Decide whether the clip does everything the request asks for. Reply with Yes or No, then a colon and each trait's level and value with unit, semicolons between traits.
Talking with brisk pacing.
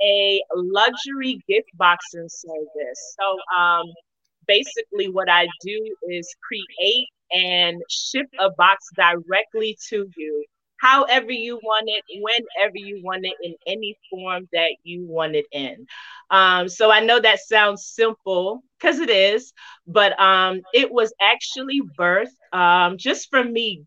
No: average, 140 wpm